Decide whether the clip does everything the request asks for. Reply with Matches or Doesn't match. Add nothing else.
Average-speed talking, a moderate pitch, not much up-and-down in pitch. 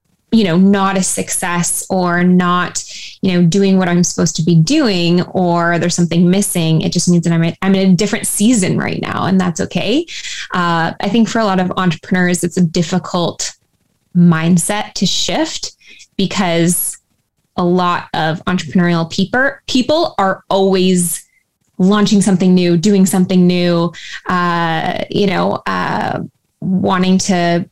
Matches